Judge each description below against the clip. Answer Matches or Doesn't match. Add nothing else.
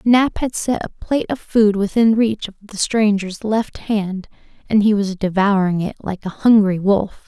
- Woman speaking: Matches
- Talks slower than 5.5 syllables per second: Matches